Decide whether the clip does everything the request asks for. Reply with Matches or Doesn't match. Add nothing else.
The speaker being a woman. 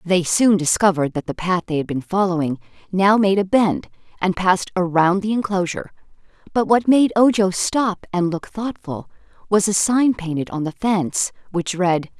Matches